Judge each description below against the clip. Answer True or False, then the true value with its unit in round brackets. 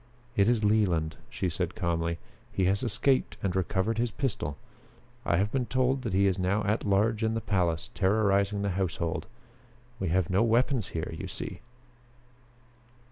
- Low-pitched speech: True (100 Hz)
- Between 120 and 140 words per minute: False (165 wpm)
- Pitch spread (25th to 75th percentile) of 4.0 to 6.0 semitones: False (3.5 semitones)